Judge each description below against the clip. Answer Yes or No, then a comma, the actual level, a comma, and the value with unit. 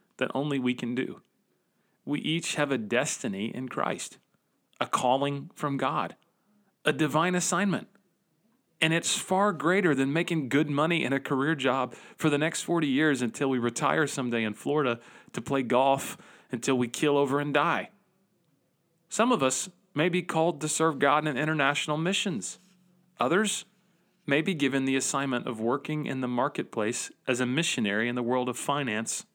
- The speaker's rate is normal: Yes, average, 170 wpm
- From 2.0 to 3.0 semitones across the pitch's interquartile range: No, average, 4.5 semitones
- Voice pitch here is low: No, medium, 150 Hz